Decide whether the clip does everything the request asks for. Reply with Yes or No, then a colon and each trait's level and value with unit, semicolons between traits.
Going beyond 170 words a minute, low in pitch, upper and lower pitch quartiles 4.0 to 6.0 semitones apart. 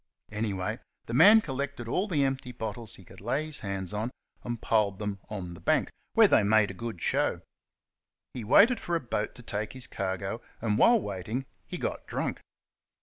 Yes: average, 190 wpm; low, 110 Hz; average, 4.8 semitones